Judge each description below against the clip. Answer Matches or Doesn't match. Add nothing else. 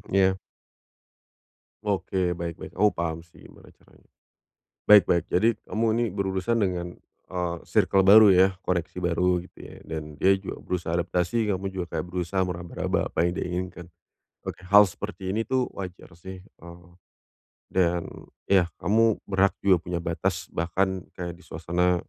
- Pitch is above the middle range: Doesn't match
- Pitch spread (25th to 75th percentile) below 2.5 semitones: Matches